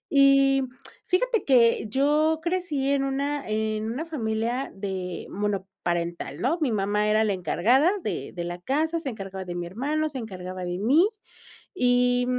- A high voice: Yes, high, 240 Hz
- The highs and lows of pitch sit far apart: Yes, wide, 6.5 semitones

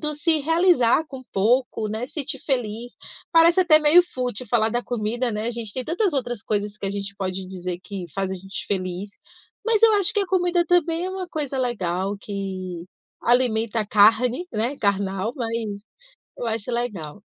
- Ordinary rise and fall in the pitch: No, wide, 6.9 semitones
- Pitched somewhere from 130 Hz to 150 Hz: No, high, 235 Hz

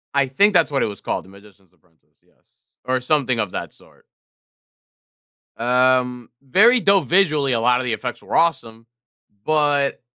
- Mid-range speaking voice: No, low, 130 Hz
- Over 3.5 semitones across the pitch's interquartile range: Yes, average, 4.7 semitones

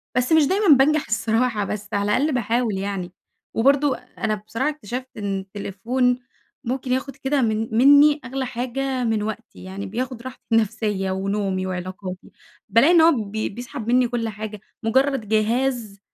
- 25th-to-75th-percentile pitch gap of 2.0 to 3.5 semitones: No, average, 4.0 semitones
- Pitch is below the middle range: No, high, 230 Hz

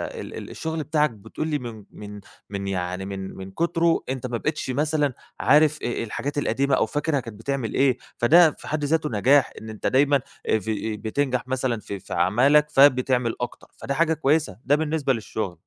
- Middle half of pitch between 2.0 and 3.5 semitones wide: No, average, 5.3 semitones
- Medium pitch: No, low, 130 Hz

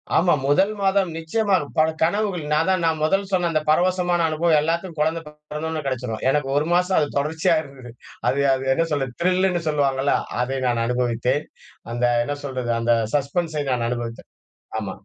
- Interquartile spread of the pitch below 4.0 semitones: No, average, 4.5 semitones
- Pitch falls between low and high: Yes, medium, 155 Hz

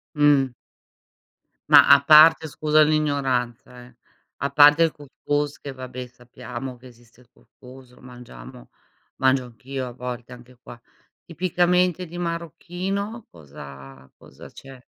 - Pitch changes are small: No, average, 3.8 semitones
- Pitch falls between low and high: No, low, 130 Hz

